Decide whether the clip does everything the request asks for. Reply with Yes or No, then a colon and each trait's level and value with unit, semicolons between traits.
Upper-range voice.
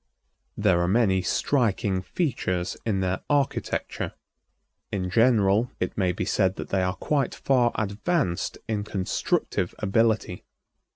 No: low, 100 Hz